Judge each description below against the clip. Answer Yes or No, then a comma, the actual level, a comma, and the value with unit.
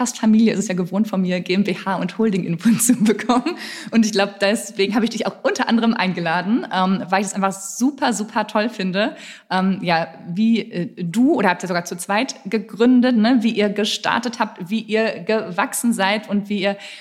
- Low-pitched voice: No, high, 205 Hz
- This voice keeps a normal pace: No, fast, 205 wpm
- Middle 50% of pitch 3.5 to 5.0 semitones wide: No, average, 2.9 semitones